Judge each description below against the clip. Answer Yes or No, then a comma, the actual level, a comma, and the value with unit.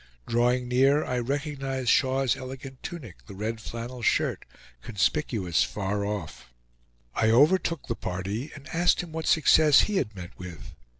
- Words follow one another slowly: No, average, 145 wpm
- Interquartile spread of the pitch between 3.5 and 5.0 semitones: No, wide, 5.4 semitones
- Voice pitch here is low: Yes, low, 125 Hz